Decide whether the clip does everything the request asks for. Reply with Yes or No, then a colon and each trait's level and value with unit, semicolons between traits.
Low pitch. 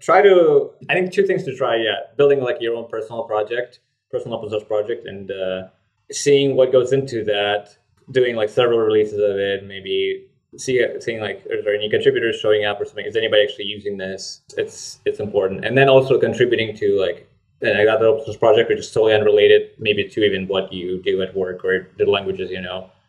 No: medium, 145 Hz